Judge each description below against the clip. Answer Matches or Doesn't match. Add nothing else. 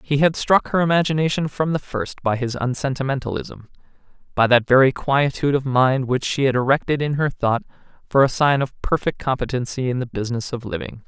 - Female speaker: Doesn't match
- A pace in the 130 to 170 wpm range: Doesn't match